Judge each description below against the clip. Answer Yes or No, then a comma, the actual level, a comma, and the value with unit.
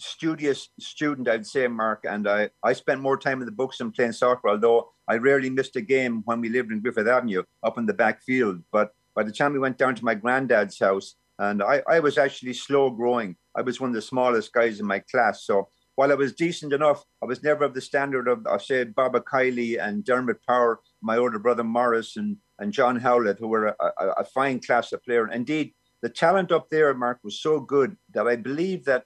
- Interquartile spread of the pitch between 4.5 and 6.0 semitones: No, average, 3.3 semitones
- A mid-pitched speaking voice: No, low, 125 Hz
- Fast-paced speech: Yes, fast, 230 wpm